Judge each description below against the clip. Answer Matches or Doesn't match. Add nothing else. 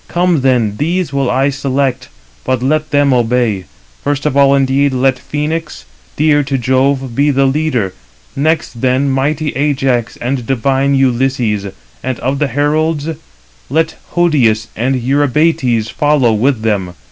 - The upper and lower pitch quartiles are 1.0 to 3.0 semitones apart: Matches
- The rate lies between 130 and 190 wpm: Matches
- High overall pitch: Doesn't match